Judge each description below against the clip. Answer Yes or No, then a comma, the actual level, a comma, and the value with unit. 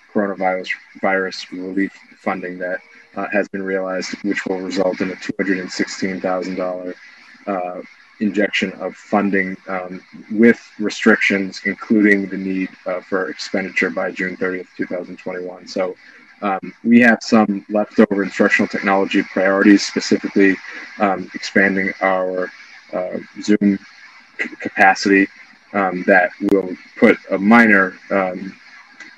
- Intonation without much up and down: Yes, narrow, 1.4 semitones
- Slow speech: Yes, slow, 115 wpm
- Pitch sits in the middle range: No, very low, 95 Hz